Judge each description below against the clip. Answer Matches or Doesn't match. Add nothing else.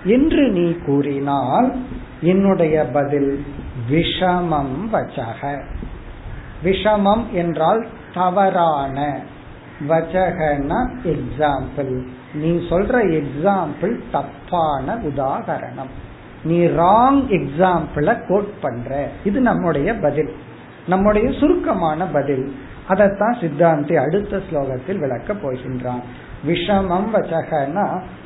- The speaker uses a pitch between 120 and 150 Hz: Doesn't match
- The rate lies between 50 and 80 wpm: Matches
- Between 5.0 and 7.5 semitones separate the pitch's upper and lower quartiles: Matches